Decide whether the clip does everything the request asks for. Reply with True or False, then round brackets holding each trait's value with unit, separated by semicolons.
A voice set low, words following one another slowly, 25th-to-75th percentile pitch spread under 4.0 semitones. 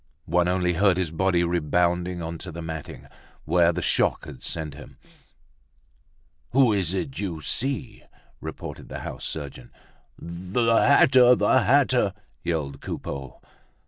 True (90 Hz; 130 wpm; 3.1 semitones)